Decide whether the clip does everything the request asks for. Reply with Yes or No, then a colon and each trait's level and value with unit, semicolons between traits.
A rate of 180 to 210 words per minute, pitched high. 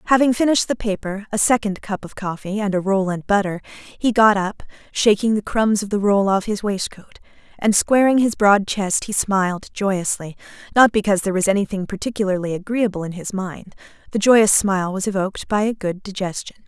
Yes: average, 185 wpm; high, 200 Hz